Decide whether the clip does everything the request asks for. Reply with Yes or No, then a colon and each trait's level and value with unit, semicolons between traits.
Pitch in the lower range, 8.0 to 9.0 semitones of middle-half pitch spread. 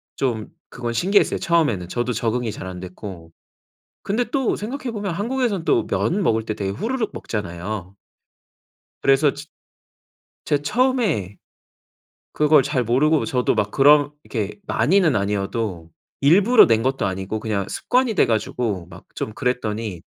Yes: low, 125 Hz; wide, 8.6 semitones